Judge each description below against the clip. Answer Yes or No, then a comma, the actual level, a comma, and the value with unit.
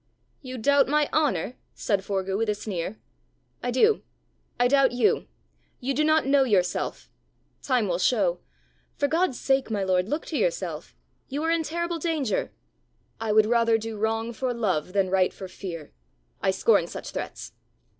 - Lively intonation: Yes, wide, 6.2 semitones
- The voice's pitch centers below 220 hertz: No, high, 235 Hz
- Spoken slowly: No, average, 165 wpm